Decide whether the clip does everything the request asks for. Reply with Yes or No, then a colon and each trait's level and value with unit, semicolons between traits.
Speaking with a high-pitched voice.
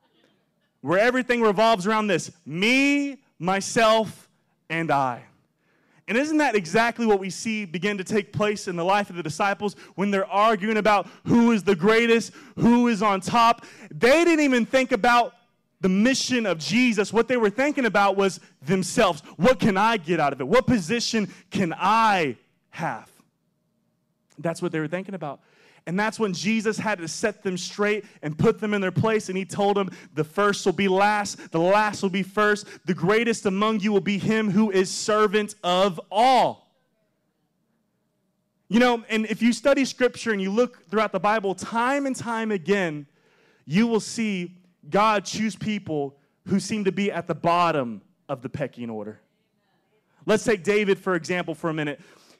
Yes: high, 205 Hz